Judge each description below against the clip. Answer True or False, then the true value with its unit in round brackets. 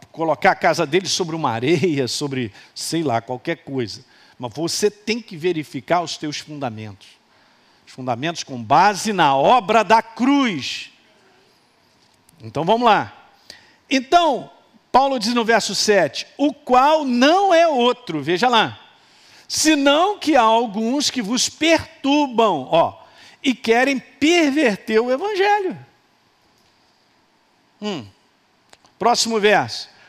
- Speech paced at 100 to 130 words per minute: True (120 wpm)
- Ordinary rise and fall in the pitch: False (8.8 semitones)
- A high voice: True (220 Hz)